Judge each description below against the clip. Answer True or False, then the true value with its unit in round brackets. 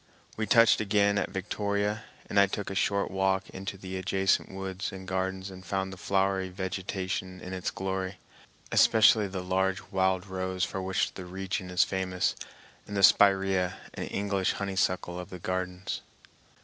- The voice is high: False (95 Hz)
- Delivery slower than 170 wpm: True (160 wpm)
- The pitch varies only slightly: True (0.9 semitones)